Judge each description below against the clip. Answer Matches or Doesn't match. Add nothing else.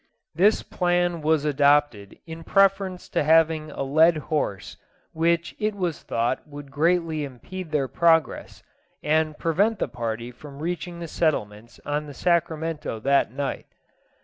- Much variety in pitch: Doesn't match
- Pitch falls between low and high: Matches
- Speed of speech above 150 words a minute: Doesn't match